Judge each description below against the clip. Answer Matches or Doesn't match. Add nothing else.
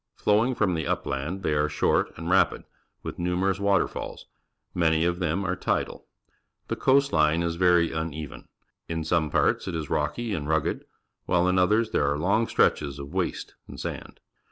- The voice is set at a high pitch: Doesn't match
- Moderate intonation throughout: Matches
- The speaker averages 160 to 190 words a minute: Matches